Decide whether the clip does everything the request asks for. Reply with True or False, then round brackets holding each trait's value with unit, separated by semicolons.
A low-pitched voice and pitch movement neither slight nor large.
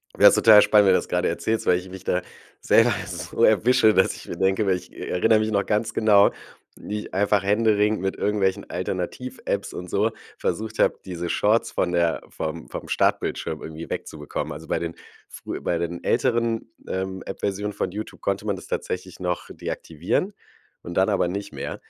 True (100 Hz; 3.1 semitones)